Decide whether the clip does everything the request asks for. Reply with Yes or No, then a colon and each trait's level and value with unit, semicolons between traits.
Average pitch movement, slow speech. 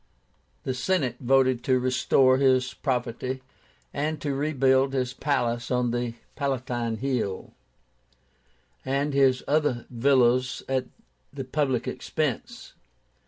No: narrow, 1.9 semitones; slow, 110 wpm